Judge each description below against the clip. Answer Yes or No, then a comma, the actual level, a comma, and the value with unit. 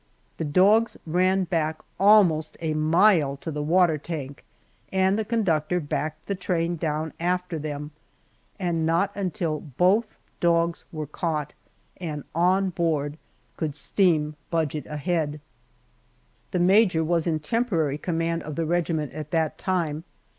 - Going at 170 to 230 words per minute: No, average, 140 wpm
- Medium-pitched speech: Yes, medium, 165 Hz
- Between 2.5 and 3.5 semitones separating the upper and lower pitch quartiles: Yes, average, 3.0 semitones